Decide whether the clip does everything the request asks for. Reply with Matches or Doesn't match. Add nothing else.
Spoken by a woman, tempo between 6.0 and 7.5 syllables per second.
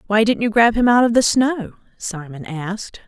Doesn't match